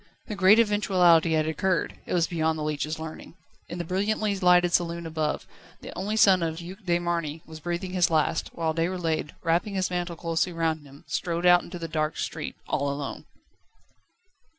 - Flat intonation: Yes, narrow, 2.3 semitones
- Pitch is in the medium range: Yes, medium, 170 Hz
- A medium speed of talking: Yes, average, 185 wpm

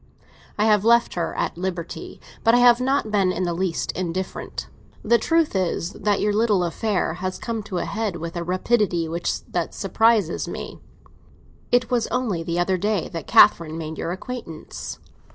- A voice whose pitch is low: No, high, 190 Hz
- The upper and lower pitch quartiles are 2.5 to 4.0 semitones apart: No, average, 4.7 semitones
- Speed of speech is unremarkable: Yes, average, 170 wpm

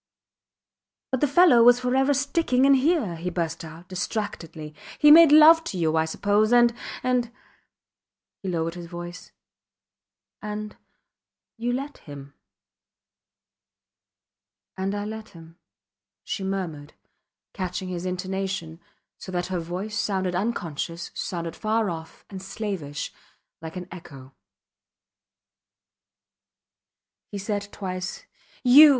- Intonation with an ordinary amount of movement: No, wide, 5.7 semitones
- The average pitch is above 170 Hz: Yes, high, 190 Hz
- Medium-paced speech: No, slow, 115 wpm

